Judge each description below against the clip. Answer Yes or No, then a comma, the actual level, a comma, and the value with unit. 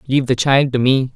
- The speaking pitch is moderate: No, low, 130 Hz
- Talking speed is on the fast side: Yes, fast, 260 wpm